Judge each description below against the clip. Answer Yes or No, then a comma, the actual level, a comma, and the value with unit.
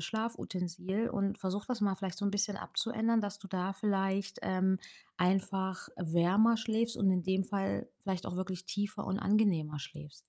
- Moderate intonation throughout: No, narrow, 1.9 semitones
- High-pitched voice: Yes, high, 195 Hz